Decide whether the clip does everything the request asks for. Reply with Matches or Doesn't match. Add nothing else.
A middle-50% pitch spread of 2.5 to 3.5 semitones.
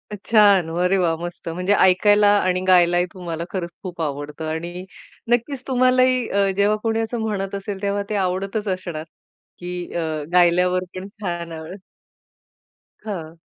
Matches